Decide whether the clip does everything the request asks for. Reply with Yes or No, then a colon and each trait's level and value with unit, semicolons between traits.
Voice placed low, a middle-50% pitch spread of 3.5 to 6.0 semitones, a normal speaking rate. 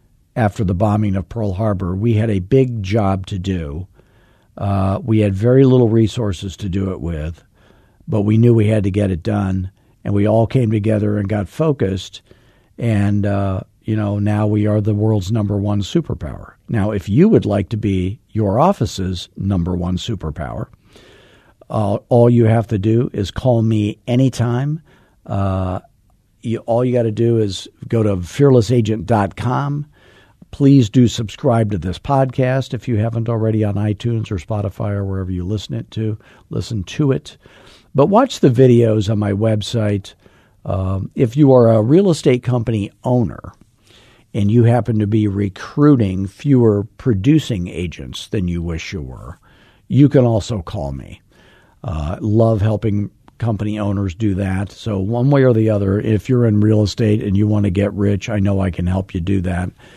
No: low, 105 Hz; average, 3.0 semitones; average, 175 wpm